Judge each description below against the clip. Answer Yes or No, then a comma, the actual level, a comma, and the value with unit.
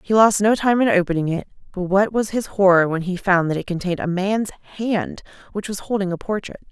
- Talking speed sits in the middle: No, fast, 230 wpm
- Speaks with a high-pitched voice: Yes, high, 195 Hz